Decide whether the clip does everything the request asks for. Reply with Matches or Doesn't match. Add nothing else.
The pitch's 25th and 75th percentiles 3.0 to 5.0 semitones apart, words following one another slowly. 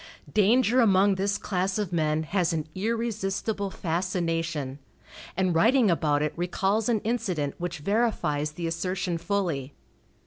Matches